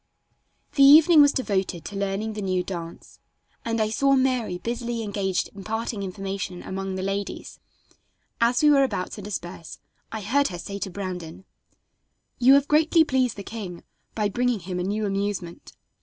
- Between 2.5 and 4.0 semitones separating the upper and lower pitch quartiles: No, average, 4.5 semitones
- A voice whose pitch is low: No, high, 205 Hz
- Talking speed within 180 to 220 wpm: No, average, 165 wpm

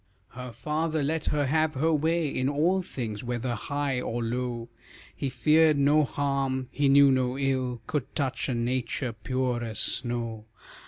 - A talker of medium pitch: No, low, 130 Hz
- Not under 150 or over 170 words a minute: Yes, average, 160 wpm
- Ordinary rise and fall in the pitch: Yes, average, 3.2 semitones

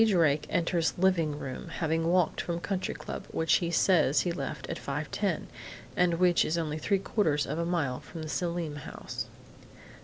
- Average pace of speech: Yes, average, 175 wpm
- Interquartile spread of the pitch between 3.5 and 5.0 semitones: No, average, 2.8 semitones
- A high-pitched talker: No, medium, 165 Hz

